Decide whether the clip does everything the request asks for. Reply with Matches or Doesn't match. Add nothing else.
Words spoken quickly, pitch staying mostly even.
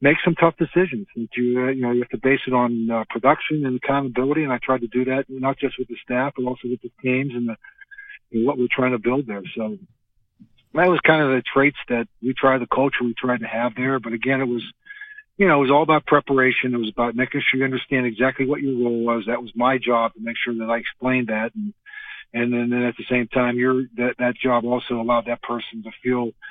Matches